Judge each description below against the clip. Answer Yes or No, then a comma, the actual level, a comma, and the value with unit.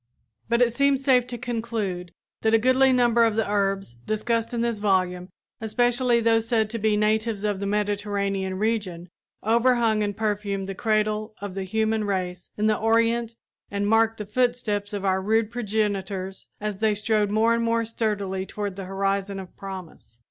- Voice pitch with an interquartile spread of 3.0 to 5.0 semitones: No, narrow, 2.6 semitones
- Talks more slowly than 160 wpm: No, average, 175 wpm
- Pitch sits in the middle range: No, high, 215 Hz